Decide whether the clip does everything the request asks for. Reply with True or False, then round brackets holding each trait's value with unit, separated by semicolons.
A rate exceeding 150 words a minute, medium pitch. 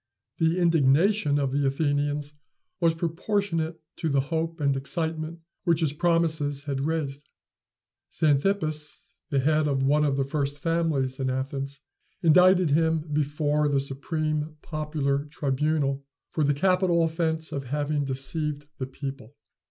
False (135 wpm; 150 Hz)